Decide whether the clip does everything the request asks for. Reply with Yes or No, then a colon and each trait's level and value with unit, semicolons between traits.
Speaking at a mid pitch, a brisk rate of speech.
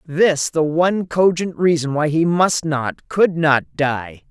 No: medium, 165 Hz; average, 165 wpm